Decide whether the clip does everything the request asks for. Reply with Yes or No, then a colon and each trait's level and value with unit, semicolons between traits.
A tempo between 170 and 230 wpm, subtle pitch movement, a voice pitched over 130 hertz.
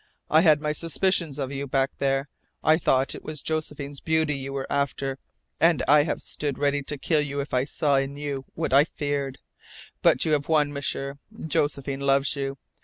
Yes: average, 190 wpm; narrow, 1.7 semitones; medium, 140 Hz